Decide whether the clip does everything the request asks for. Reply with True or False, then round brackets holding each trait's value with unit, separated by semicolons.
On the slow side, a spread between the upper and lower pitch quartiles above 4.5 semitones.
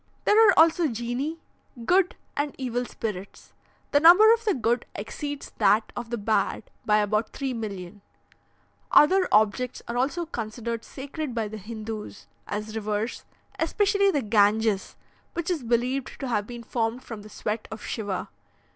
False (150 wpm; 5.2 semitones)